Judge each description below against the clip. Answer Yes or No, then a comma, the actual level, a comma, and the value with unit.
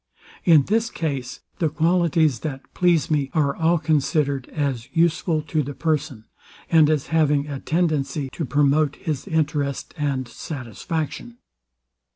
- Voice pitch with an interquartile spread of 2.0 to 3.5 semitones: Yes, average, 2.7 semitones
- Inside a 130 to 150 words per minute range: Yes, slow, 135 wpm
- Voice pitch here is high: No, medium, 150 Hz